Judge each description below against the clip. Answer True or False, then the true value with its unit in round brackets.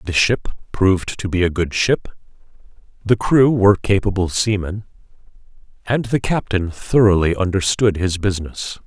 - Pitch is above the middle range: False (95 Hz)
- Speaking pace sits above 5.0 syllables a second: False (4.8 syllables/s)